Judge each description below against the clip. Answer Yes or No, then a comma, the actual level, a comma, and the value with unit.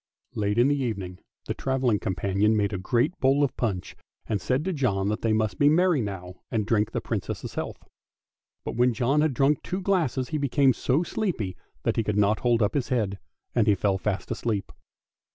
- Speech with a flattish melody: No, average, 5.1 semitones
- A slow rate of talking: No, fast, 205 wpm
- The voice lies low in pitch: Yes, low, 115 Hz